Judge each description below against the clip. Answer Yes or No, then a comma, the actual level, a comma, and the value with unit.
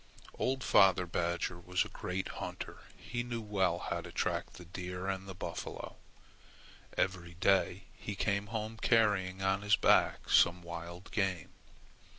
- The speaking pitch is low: Yes, very low, 95 Hz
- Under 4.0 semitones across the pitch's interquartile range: Yes, narrow, 2.6 semitones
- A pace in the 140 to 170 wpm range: Yes, average, 145 wpm